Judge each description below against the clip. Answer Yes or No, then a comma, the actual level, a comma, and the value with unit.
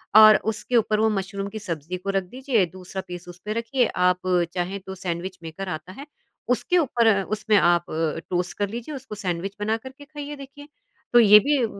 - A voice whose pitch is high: Yes, high, 205 Hz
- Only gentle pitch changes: No, average, 4.6 semitones